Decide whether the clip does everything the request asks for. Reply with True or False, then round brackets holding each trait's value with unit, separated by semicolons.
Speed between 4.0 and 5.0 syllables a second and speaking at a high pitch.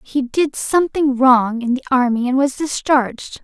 True (4.6 syllables/s; 265 Hz)